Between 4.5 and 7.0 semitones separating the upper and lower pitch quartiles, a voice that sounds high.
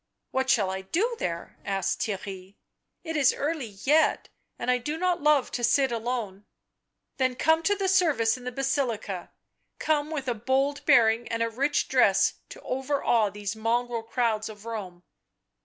Yes: average, 4.9 semitones; high, 245 Hz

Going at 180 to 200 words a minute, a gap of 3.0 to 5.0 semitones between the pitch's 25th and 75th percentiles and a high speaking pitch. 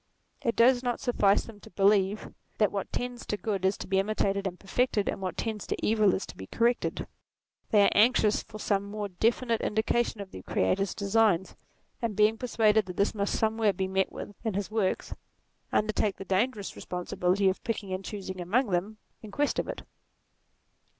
No: average, 190 wpm; narrow, 2.5 semitones; high, 205 Hz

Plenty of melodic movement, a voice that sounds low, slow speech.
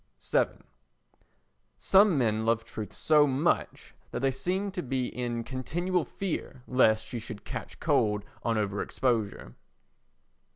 Yes: wide, 5.8 semitones; low, 125 Hz; slow, 130 wpm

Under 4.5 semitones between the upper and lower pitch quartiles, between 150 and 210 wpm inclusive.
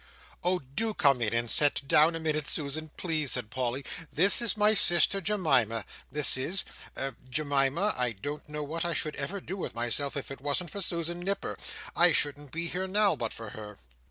No: average, 4.8 semitones; average, 190 wpm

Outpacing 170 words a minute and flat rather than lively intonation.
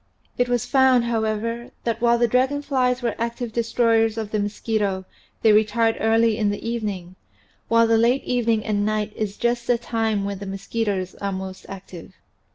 Yes: average, 180 wpm; narrow, 2.3 semitones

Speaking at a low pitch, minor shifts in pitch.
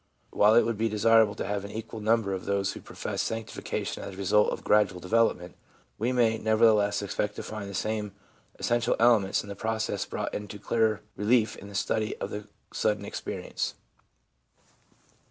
Yes: low, 105 Hz; narrow, 1.9 semitones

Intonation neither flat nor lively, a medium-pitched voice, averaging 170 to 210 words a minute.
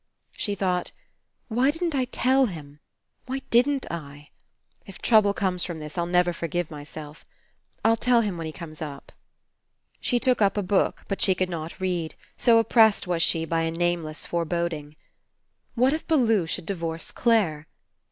No: wide, 5.7 semitones; medium, 180 Hz; average, 175 wpm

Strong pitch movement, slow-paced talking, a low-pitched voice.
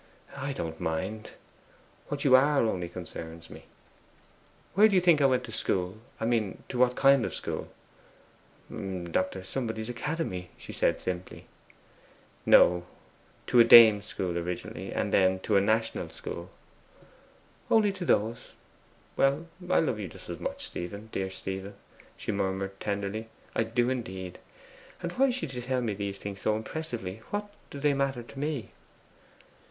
No: wide, 6.2 semitones; average, 155 wpm; low, 110 Hz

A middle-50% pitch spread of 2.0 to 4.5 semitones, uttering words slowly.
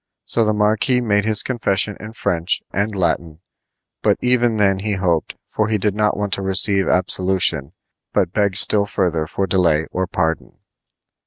No: average, 2.8 semitones; average, 165 wpm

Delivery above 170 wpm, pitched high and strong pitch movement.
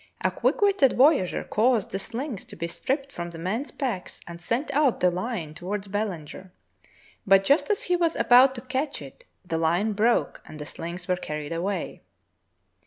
Yes: average, 180 wpm; high, 205 Hz; wide, 7.3 semitones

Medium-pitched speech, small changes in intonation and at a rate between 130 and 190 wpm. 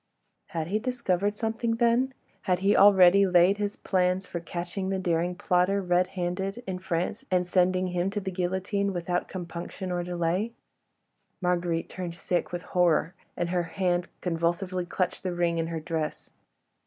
Yes: medium, 180 Hz; narrow, 1.9 semitones; average, 160 wpm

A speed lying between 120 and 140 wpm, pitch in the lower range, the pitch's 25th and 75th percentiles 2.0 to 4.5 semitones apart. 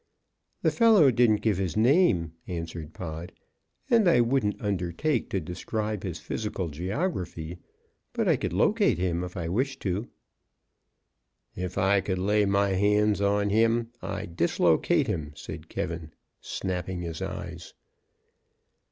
Yes: slow, 135 wpm; very low, 95 Hz; average, 4.0 semitones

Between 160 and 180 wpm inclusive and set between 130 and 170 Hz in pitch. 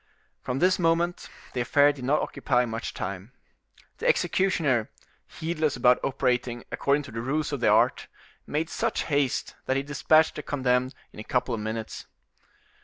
Yes: average, 165 wpm; low, 135 Hz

